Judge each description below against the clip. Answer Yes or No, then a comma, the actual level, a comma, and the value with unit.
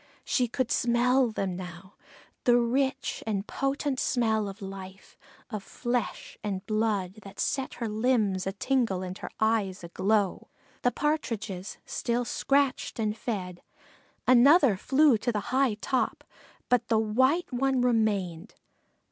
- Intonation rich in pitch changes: No, average, 4.5 semitones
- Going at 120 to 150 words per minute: Yes, average, 140 wpm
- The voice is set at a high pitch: Yes, high, 225 Hz